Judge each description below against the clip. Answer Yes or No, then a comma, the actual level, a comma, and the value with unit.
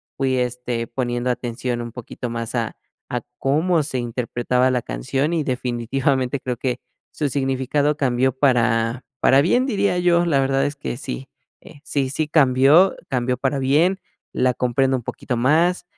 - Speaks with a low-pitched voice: Yes, low, 130 Hz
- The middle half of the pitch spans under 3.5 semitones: Yes, average, 2.8 semitones